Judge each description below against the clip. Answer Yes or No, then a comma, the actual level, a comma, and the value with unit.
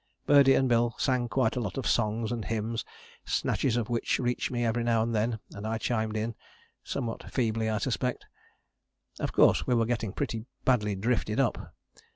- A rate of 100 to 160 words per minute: No, average, 185 wpm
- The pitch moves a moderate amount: No, narrow, 1.8 semitones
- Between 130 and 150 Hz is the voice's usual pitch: No, low, 115 Hz